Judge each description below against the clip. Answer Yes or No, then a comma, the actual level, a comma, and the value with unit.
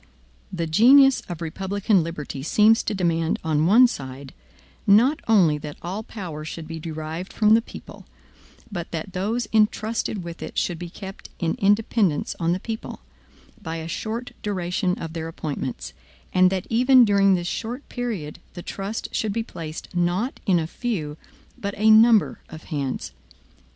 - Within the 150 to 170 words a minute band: Yes, average, 160 wpm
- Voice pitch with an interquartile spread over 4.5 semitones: Yes, average, 5.0 semitones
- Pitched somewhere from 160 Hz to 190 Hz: Yes, medium, 185 Hz